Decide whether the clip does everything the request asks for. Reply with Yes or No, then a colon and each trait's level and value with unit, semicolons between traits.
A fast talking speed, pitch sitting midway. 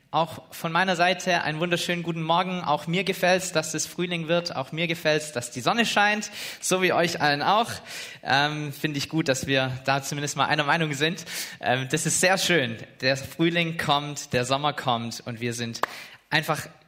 Yes: fast, 200 wpm; medium, 155 Hz